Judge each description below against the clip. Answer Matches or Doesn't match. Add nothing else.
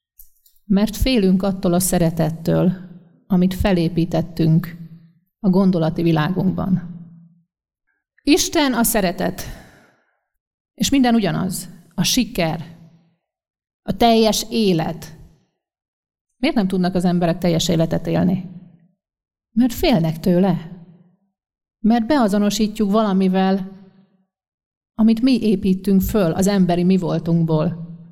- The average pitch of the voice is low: Doesn't match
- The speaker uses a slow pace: Matches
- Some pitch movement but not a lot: Matches